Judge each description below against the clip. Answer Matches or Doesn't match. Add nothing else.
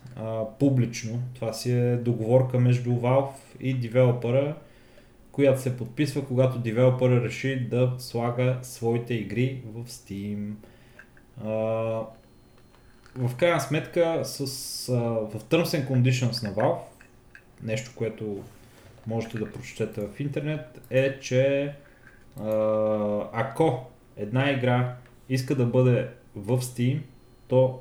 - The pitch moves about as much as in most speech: Doesn't match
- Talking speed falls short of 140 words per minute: Matches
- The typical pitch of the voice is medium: Doesn't match